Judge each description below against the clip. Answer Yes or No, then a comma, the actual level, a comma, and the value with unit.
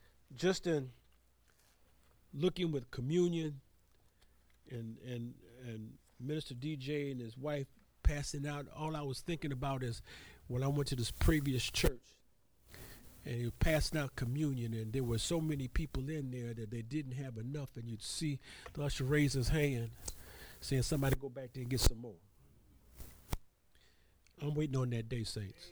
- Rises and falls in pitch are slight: No, average, 4.4 semitones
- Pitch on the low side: Yes, low, 130 Hz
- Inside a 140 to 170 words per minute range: Yes, average, 165 wpm